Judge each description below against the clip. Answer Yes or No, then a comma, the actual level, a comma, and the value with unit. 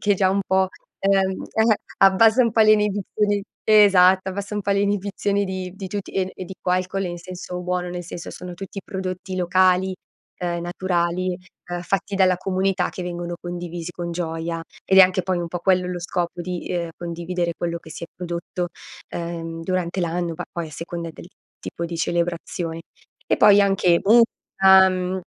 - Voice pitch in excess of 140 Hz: Yes, medium, 185 Hz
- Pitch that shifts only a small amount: Yes, narrow, 2.0 semitones